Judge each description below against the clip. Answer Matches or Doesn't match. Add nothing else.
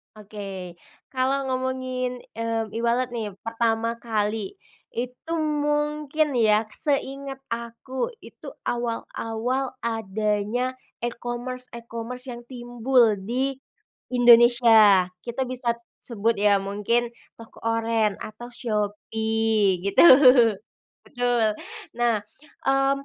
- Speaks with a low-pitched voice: Doesn't match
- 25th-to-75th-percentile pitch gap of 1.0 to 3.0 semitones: Matches